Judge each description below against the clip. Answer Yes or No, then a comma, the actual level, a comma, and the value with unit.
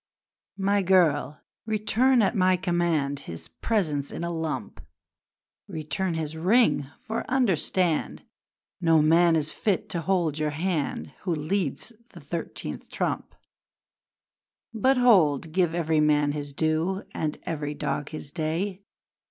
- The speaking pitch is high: No, medium, 165 Hz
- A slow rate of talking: Yes, slow, 125 wpm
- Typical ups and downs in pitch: Yes, average, 4.0 semitones